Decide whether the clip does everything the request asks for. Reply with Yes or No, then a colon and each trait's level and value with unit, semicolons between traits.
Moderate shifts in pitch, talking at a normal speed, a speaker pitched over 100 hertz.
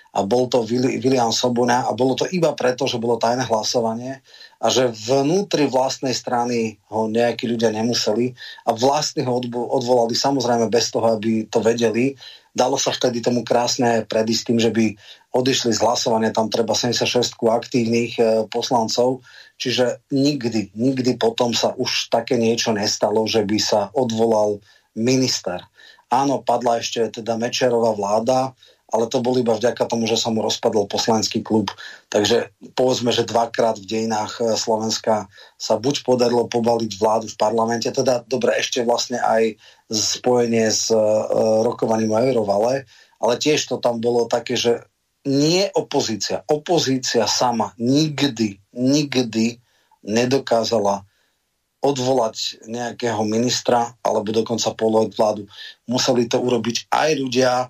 No: narrow, 2.1 semitones; average, 140 wpm; low, 120 Hz